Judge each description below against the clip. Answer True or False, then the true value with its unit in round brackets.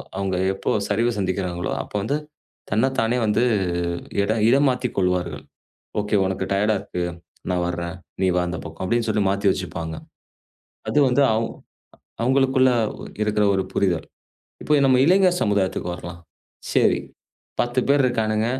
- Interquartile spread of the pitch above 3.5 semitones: True (4.7 semitones)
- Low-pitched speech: True (105 Hz)